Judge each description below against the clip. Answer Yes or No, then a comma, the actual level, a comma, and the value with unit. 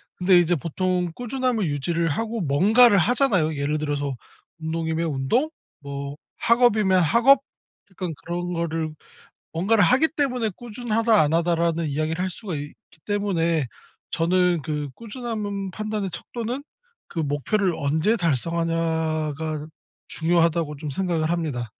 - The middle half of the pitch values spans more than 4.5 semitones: Yes, average, 5.2 semitones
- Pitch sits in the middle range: Yes, medium, 170 Hz